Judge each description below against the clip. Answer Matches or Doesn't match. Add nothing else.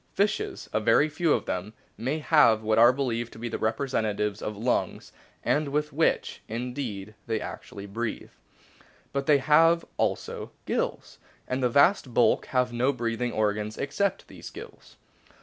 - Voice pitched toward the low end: Matches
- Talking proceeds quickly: Doesn't match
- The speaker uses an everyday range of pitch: Matches